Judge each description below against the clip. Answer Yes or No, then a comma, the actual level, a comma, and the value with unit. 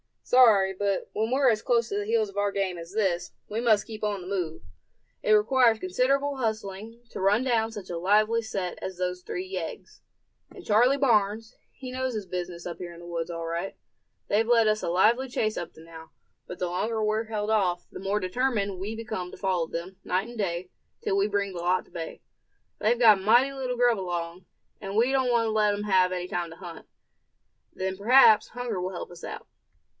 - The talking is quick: Yes, fast, 215 wpm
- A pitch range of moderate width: Yes, average, 3.9 semitones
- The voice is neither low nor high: No, high, 205 Hz